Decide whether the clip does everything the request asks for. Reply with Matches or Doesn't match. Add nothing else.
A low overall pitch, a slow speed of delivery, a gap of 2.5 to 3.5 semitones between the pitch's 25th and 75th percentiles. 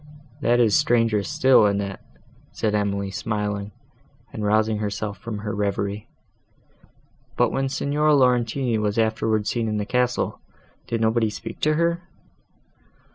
Matches